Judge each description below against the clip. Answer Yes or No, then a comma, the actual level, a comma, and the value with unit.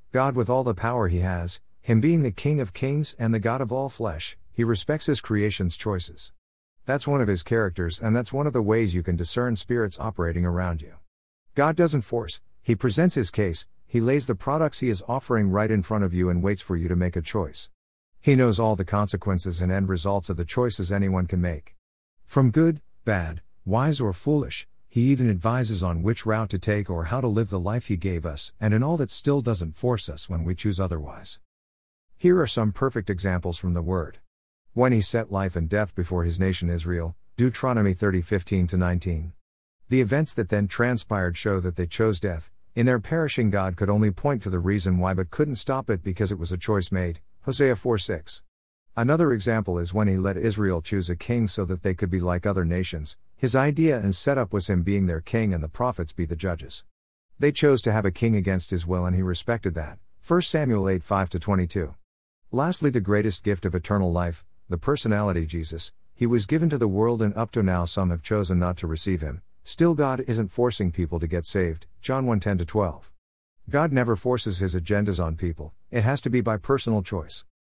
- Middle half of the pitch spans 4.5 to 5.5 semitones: Yes, average, 5.1 semitones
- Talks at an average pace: No, fast, 215 wpm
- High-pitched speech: No, low, 100 Hz